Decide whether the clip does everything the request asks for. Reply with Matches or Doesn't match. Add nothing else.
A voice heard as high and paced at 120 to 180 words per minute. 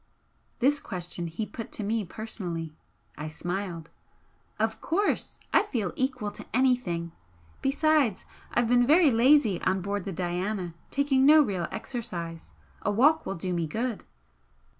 Matches